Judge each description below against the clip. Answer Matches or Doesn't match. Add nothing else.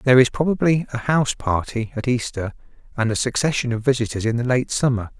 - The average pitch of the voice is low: Matches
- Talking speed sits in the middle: Matches